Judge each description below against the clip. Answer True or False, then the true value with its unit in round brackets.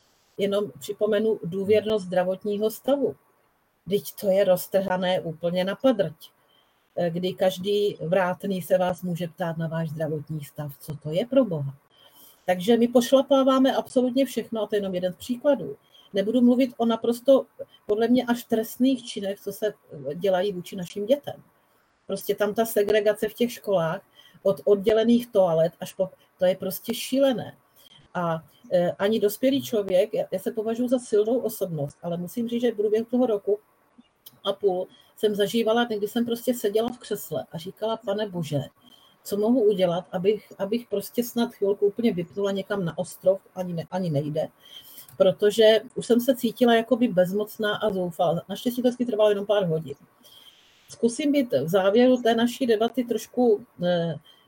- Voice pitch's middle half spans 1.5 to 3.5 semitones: False (4.1 semitones)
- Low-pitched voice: False (205 Hz)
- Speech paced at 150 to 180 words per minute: True (160 wpm)